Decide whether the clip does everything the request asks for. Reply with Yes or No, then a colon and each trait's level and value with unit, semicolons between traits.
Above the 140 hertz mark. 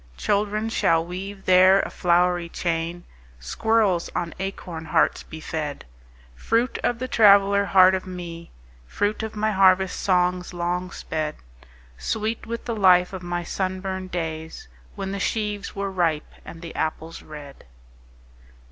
Yes: medium, 185 Hz